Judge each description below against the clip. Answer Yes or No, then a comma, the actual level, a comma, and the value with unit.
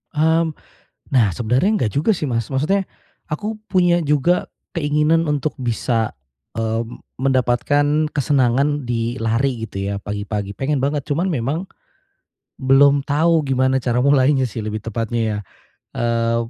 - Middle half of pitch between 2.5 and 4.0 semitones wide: No, average, 4.4 semitones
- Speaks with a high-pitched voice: No, low, 135 Hz